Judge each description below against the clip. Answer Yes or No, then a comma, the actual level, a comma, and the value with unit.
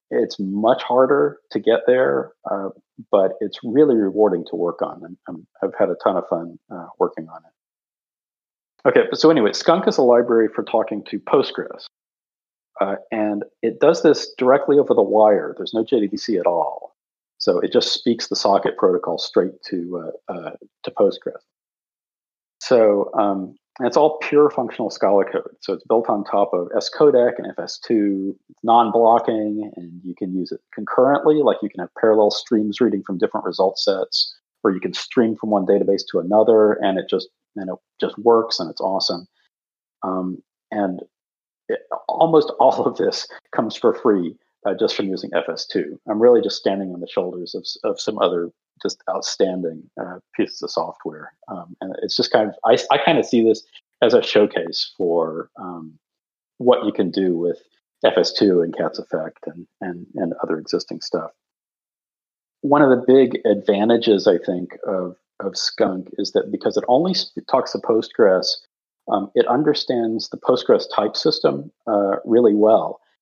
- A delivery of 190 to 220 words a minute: No, average, 175 wpm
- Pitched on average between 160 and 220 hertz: No, low, 120 Hz